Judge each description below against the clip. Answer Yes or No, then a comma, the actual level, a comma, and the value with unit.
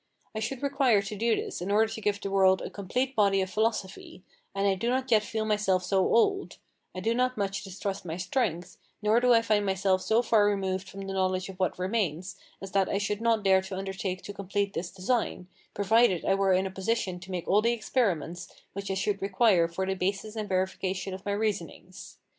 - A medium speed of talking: No, fast, 225 wpm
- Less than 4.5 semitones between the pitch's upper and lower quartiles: Yes, narrow, 2.6 semitones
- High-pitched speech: Yes, high, 195 Hz